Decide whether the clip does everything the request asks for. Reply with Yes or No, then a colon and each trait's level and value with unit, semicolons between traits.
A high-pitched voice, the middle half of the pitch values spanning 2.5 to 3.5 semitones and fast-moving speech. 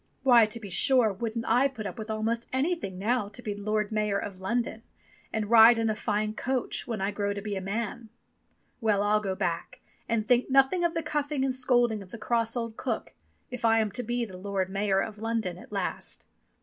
Yes: high, 220 Hz; average, 2.9 semitones; fast, 215 wpm